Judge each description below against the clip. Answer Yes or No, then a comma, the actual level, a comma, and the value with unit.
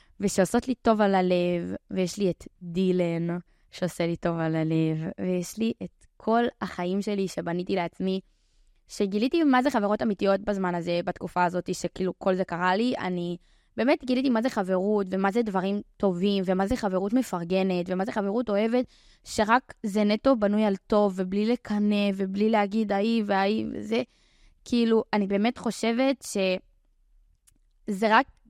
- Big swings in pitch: No, average, 3.5 semitones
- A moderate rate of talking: No, fast, 155 wpm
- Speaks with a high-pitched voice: Yes, high, 200 Hz